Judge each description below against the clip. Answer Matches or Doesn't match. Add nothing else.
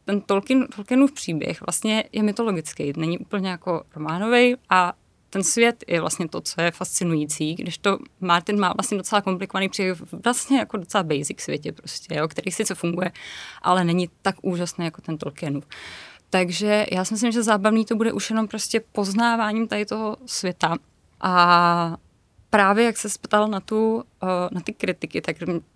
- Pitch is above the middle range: Matches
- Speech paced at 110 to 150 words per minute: Doesn't match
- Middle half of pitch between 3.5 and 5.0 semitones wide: Matches